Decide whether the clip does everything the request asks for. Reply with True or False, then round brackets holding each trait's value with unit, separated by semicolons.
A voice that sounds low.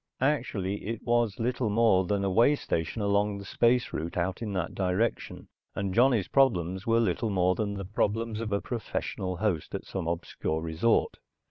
True (100 Hz)